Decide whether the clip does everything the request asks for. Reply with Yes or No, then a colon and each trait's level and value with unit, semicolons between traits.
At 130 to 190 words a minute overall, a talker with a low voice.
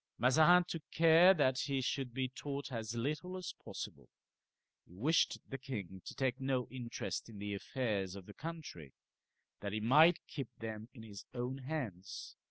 Yes: average, 170 wpm; low, 130 Hz